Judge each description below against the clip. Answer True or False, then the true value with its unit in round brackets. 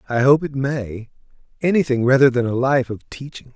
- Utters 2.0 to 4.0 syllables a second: False (5.2 syllables/s)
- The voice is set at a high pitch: False (130 Hz)